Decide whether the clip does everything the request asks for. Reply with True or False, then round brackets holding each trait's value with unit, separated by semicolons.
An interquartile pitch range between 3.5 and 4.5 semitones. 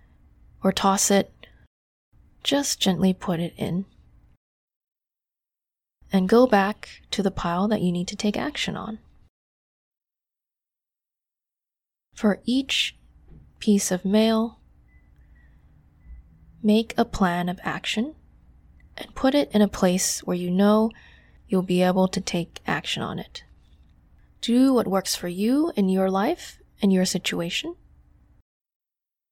True (3.8 semitones)